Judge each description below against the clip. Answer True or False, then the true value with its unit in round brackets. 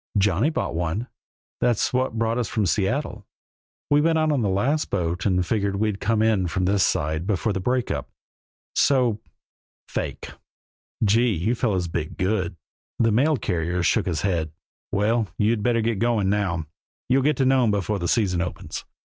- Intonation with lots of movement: False (4.5 semitones)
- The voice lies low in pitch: True (105 Hz)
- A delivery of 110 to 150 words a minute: False (170 wpm)